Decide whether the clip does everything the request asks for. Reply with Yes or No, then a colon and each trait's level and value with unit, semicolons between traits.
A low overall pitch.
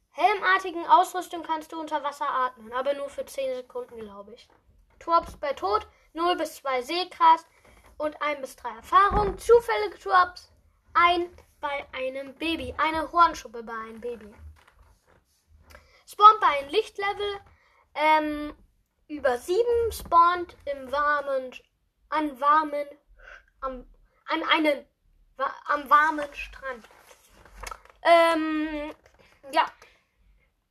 No: very high, 300 Hz